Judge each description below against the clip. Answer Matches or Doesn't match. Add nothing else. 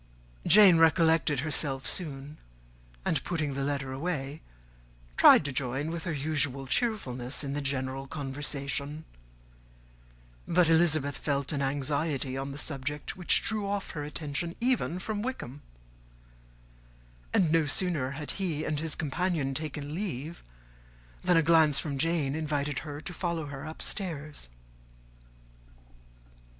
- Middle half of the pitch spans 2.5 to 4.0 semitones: Matches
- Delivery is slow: Matches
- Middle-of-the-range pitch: Matches